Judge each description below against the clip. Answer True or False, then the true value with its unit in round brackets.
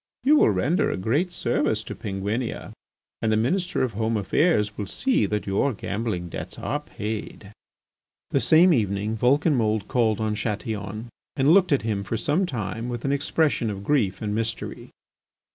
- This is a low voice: True (115 Hz)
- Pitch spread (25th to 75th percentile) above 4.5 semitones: True (5.1 semitones)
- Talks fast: False (165 wpm)